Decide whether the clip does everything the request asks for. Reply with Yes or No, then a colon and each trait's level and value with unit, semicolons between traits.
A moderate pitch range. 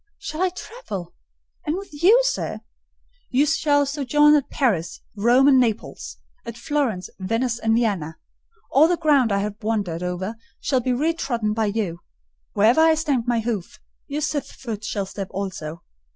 No: wide, 6.6 semitones